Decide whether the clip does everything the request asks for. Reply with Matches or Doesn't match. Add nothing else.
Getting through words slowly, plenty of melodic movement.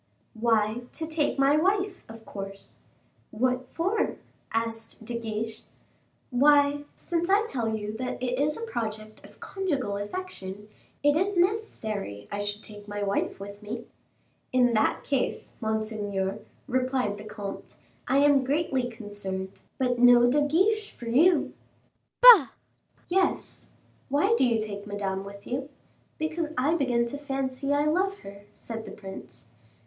Doesn't match